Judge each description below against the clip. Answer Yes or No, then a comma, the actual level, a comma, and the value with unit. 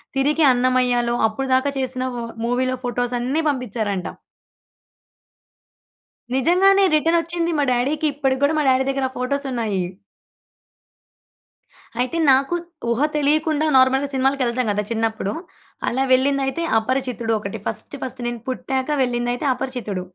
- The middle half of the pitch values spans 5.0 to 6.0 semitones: No, narrow, 2.6 semitones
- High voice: Yes, very high, 260 Hz